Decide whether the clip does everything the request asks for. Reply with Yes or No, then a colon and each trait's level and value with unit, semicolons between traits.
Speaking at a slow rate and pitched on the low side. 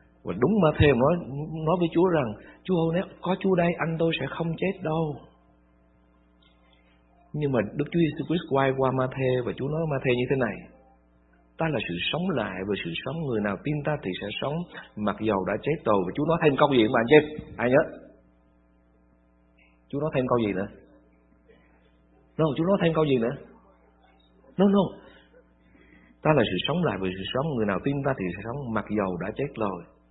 No: average, 210 wpm; low, 115 Hz